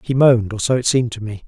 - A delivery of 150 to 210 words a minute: No, fast, 325 wpm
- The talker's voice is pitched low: Yes, low, 120 Hz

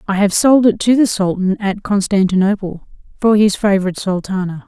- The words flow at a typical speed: Yes, average, 165 wpm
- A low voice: No, high, 200 Hz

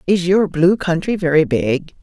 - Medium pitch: Yes, medium, 170 Hz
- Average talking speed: Yes, average, 180 wpm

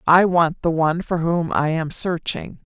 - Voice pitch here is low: No, medium, 165 Hz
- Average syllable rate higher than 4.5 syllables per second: No, 4.4 syllables/s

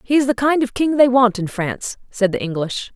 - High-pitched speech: Yes, high, 235 Hz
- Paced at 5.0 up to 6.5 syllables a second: Yes, 5.5 syllables/s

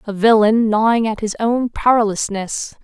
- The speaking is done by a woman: Yes, female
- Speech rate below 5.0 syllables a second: Yes, 4.6 syllables/s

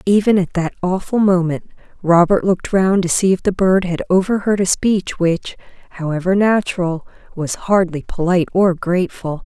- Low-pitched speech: No, medium, 185 Hz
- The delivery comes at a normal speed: Yes, average, 160 wpm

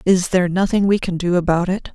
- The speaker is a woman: Yes, female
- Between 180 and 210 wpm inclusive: No, fast, 245 wpm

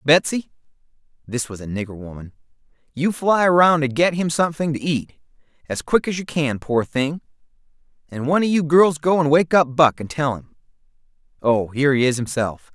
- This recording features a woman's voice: No, male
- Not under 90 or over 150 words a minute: No, average, 190 wpm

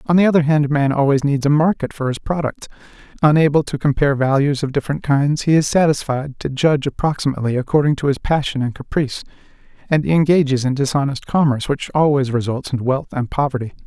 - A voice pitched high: No, medium, 140 Hz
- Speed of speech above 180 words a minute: Yes, average, 190 wpm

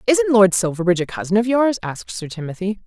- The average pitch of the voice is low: No, high, 205 Hz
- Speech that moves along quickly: Yes, fast, 210 wpm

